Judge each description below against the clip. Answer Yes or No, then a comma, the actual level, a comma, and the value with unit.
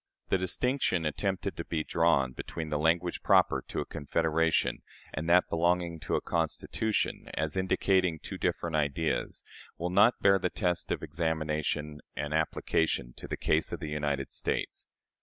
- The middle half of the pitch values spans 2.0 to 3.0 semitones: Yes, average, 2.7 semitones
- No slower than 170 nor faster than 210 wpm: No, average, 160 wpm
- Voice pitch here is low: Yes, very low, 80 Hz